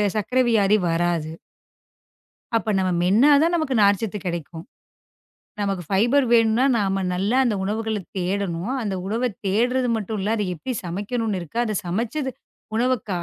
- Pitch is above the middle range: Yes, high, 210 Hz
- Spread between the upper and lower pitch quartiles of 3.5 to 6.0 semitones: Yes, average, 3.8 semitones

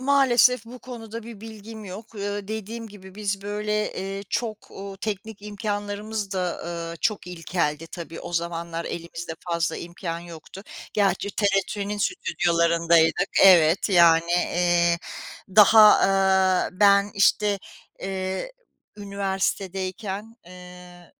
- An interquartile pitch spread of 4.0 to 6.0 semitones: No, average, 3.3 semitones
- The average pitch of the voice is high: Yes, high, 195 Hz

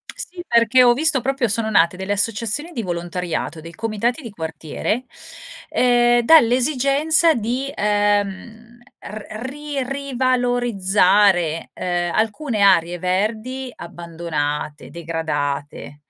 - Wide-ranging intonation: Yes, wide, 6.3 semitones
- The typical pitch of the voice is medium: No, high, 215 Hz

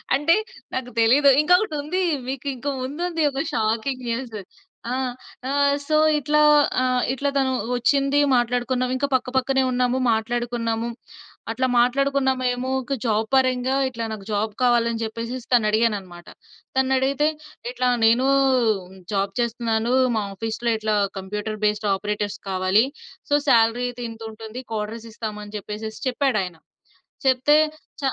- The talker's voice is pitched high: Yes, high, 240 Hz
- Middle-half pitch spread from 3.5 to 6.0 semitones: No, average, 3.1 semitones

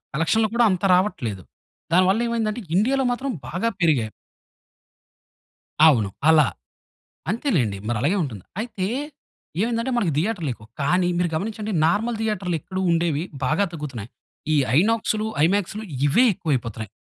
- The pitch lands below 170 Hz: No, medium, 185 Hz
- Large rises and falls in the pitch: Yes, wide, 6.7 semitones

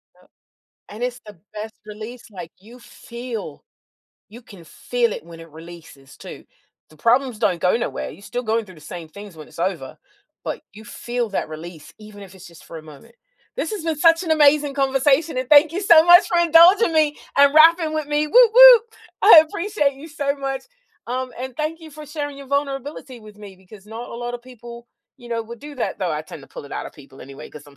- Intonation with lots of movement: Yes, wide, 7.3 semitones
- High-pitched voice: Yes, high, 245 Hz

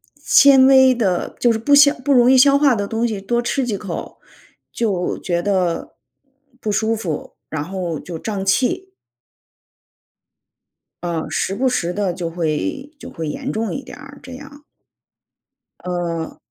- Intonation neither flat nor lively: No, wide, 6.9 semitones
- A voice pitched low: No, high, 215 Hz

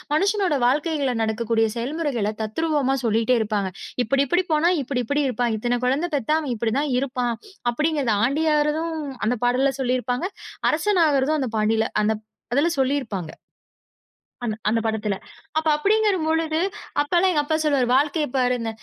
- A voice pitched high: Yes, very high, 265 Hz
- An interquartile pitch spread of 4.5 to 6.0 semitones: Yes, average, 5.0 semitones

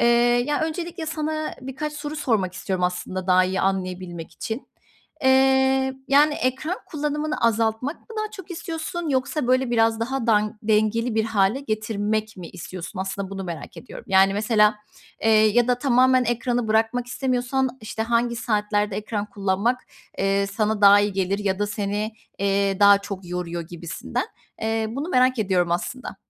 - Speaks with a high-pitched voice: Yes, high, 220 Hz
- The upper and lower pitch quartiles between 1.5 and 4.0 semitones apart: No, average, 4.8 semitones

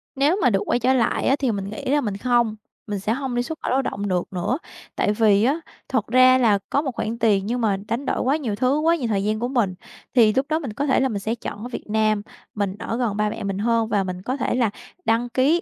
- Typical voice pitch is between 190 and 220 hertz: No, high, 230 Hz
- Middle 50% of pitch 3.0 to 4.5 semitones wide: Yes, average, 3.9 semitones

